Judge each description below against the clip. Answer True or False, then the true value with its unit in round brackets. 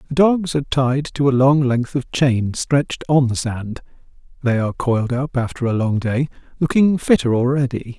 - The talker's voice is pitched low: True (130 Hz)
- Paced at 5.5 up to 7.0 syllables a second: False (5.0 syllables/s)